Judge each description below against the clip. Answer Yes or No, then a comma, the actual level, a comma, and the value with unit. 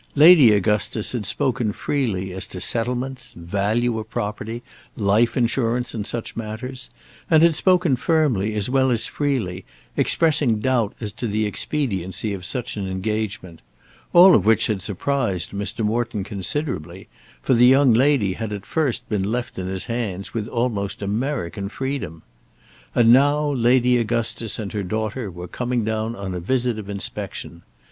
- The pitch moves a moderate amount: Yes, average, 4.1 semitones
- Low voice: Yes, low, 115 Hz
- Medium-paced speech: Yes, average, 155 wpm